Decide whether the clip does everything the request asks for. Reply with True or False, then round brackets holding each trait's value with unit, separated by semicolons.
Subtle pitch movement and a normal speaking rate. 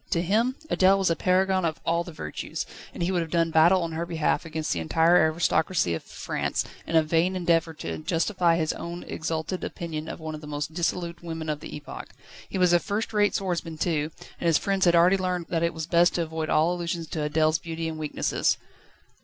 False (1.9 semitones; 220 wpm)